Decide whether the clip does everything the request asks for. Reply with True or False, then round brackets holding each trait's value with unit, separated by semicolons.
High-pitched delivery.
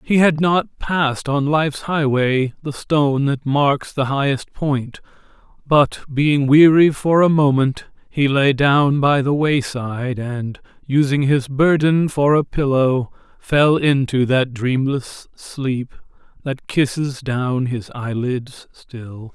False (140 Hz)